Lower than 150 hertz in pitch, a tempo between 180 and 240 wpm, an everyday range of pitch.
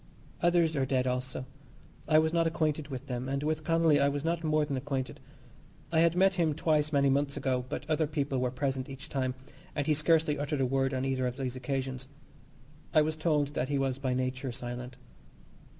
Yes: medium, 140 Hz; fast, 205 wpm; average, 3.1 semitones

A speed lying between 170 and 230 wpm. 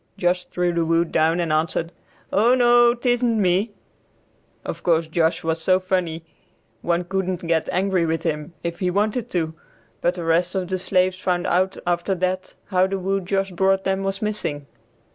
Yes: average, 180 wpm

